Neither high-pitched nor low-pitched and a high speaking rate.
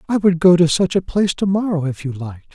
Yes: medium, 170 Hz; fast, 285 wpm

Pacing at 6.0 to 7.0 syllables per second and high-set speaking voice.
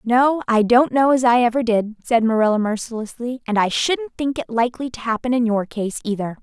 No: 5.4 syllables/s; high, 235 Hz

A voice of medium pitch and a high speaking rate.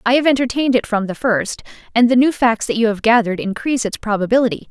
No: high, 235 Hz; fast, 230 wpm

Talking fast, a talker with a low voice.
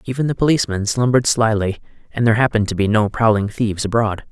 No: average, 195 wpm; low, 110 Hz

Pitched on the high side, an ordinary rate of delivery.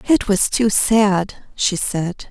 Yes: high, 205 Hz; average, 155 wpm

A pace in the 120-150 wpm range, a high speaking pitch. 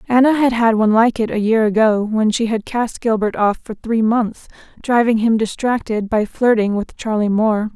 No: average, 200 wpm; high, 225 Hz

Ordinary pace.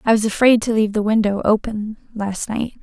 No: fast, 210 wpm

